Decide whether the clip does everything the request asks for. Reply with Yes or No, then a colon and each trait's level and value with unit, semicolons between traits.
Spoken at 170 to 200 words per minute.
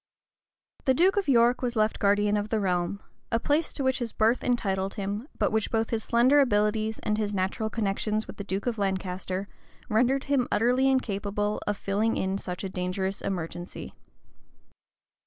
Yes: average, 175 wpm